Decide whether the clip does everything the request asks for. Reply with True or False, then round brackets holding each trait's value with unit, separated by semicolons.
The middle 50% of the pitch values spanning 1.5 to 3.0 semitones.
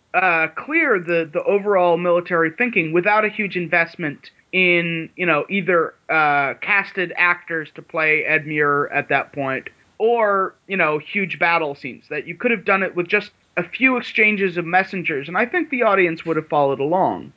False (3.6 semitones)